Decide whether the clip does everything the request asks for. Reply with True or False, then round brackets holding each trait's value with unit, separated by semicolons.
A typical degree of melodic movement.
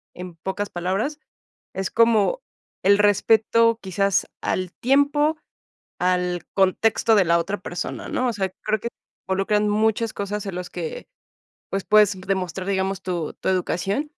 True (3.2 semitones)